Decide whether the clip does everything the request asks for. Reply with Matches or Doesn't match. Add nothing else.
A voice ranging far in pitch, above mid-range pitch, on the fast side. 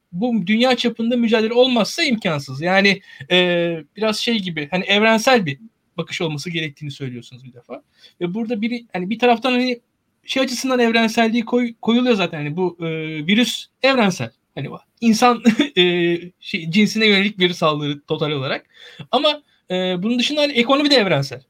Matches